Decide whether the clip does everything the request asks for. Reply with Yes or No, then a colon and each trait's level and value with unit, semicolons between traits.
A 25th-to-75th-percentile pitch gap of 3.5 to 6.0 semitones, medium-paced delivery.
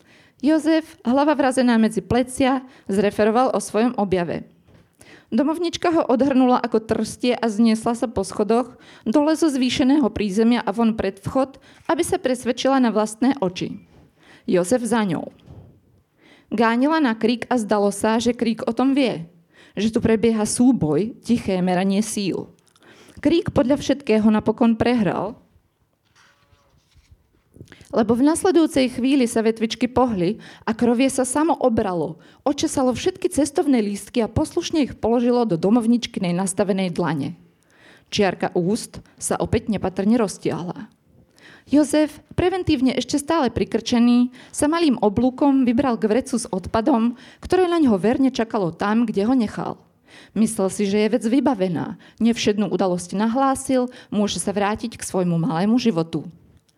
Yes: average, 4.3 semitones; average, 135 wpm